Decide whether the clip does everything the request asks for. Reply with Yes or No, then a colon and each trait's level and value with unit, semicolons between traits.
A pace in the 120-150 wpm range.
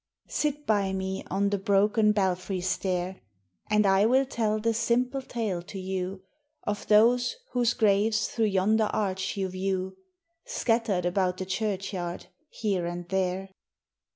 Yes: average, 140 wpm